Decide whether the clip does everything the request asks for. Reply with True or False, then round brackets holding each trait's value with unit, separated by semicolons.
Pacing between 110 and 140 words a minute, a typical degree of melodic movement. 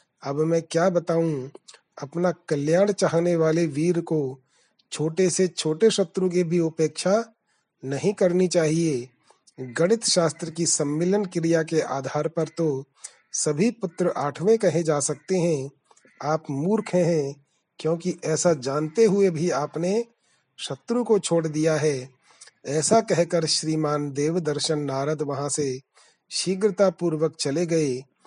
True (130 wpm; 3.2 semitones)